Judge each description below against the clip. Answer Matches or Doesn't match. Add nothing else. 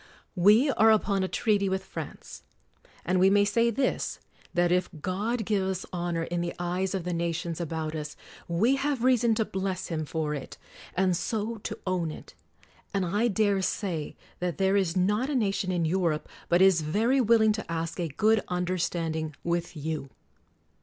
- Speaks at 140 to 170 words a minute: Doesn't match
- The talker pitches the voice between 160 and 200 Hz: Matches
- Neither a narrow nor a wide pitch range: Matches